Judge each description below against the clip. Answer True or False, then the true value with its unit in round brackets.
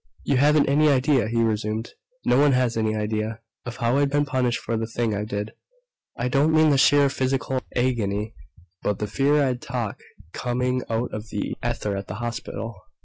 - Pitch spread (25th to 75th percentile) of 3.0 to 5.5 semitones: True (3.8 semitones)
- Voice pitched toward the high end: False (120 Hz)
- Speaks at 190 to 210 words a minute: True (195 wpm)